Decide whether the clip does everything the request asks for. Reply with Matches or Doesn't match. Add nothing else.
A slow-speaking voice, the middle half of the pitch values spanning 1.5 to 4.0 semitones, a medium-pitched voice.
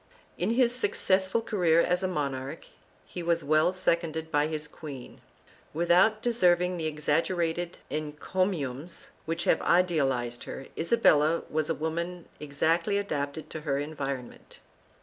Matches